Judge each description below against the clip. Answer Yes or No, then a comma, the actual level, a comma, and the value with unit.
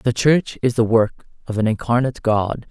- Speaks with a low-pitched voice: Yes, low, 120 Hz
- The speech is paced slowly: No, average, 200 wpm